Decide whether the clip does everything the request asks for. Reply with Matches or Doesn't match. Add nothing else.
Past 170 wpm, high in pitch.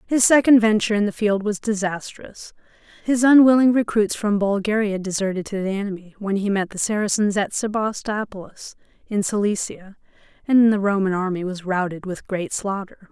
Doesn't match